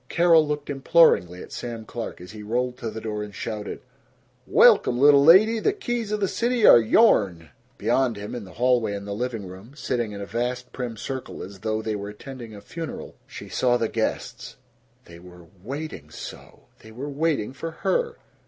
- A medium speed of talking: Yes, average, 190 wpm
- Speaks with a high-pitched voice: No, low, 120 Hz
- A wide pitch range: Yes, wide, 5.9 semitones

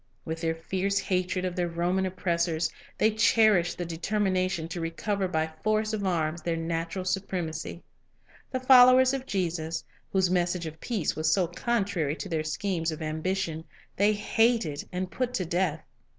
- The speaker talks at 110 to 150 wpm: No, average, 165 wpm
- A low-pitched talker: No, medium, 180 Hz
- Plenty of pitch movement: No, average, 3.5 semitones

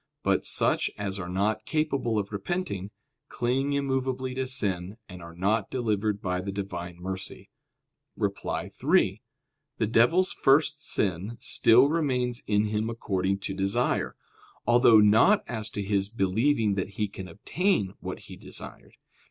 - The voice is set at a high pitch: No, low, 105 Hz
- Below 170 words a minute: Yes, average, 145 wpm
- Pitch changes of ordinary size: Yes, average, 4.7 semitones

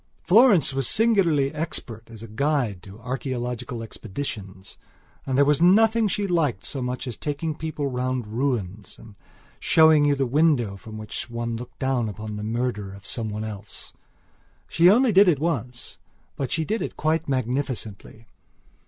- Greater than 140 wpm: Yes, average, 165 wpm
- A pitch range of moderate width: No, wide, 5.8 semitones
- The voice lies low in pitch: Yes, low, 130 Hz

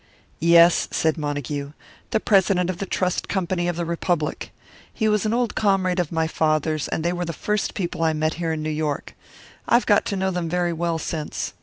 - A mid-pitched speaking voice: Yes, medium, 170 Hz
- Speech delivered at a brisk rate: Yes, fast, 210 wpm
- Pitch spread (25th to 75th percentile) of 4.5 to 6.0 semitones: No, average, 2.9 semitones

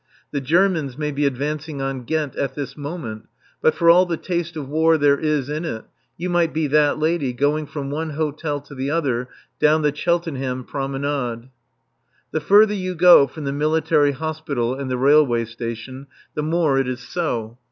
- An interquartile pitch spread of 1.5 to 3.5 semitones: Yes, average, 2.9 semitones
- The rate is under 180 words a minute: No, average, 185 wpm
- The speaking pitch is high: No, medium, 145 Hz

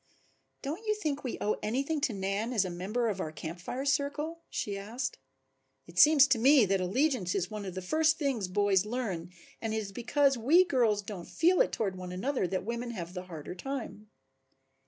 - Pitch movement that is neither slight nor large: No, wide, 6.5 semitones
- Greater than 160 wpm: Yes, average, 200 wpm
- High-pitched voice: Yes, high, 220 Hz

